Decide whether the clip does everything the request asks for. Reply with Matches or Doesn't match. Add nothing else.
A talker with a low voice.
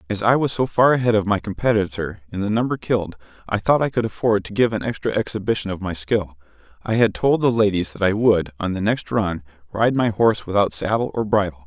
Matches